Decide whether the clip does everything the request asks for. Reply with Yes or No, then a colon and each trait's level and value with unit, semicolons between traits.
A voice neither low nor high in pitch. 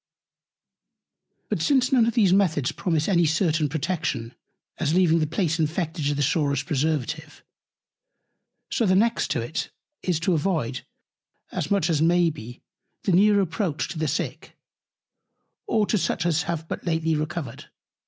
Yes: medium, 165 Hz